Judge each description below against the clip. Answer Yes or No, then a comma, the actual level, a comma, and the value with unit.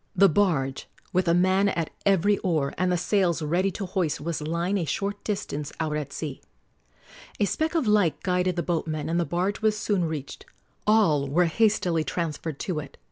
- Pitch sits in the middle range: Yes, medium, 175 Hz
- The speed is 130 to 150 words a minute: No, average, 190 wpm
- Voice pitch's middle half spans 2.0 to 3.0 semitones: No, average, 3.9 semitones